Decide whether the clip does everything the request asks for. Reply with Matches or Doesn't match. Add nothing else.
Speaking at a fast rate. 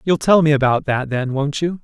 Matches